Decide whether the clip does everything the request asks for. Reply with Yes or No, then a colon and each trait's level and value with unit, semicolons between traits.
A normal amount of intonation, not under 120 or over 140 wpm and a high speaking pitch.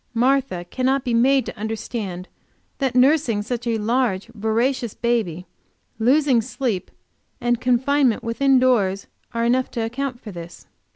Yes: average, 3.0 semitones; slow, 135 wpm; high, 240 Hz